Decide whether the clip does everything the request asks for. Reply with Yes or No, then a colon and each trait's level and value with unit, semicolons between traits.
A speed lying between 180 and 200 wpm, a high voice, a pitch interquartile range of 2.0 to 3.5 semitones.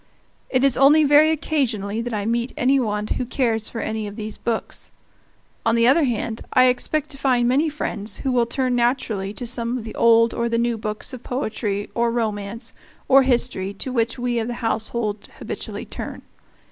Yes: average, 195 wpm; high, 235 Hz; narrow, 2.6 semitones